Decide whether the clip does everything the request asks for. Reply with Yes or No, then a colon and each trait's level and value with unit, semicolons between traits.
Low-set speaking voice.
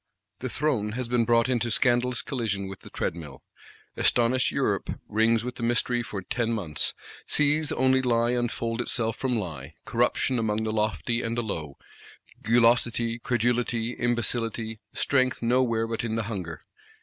Yes: low, 115 Hz